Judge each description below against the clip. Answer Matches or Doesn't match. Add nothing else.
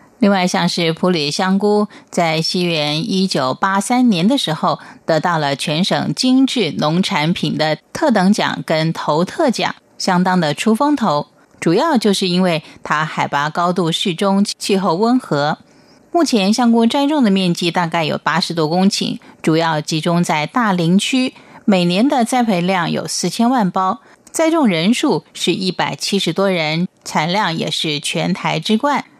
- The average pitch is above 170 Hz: Matches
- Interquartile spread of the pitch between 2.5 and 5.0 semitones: Doesn't match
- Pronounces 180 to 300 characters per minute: Matches